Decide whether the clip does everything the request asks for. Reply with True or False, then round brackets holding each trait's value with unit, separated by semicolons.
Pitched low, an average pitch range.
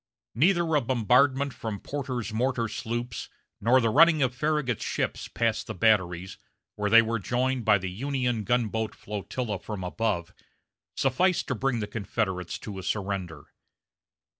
True (115 Hz; 4.1 semitones)